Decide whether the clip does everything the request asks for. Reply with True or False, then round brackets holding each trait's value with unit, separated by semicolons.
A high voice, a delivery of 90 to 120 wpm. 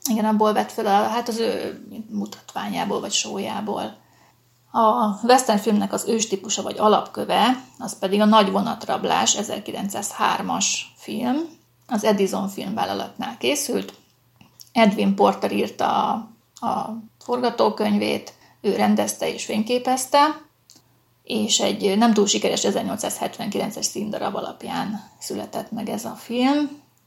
True (220 Hz; 115 wpm)